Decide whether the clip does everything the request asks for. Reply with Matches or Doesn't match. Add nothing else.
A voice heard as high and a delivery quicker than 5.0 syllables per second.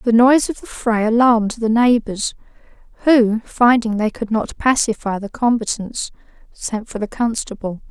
Doesn't match